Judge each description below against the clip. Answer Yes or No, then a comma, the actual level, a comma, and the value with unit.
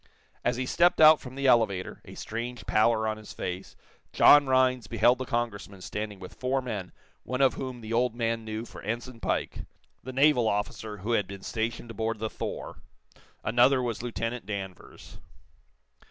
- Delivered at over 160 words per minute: Yes, average, 170 wpm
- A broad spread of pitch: No, average, 2.9 semitones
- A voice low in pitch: Yes, low, 115 Hz